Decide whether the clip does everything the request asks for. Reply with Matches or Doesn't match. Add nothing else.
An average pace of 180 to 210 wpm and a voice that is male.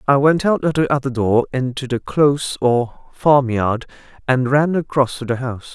Matches